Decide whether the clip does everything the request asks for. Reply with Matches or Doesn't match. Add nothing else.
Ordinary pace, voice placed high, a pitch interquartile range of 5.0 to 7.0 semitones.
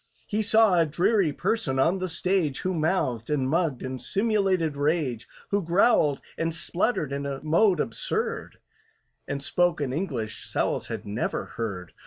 Doesn't match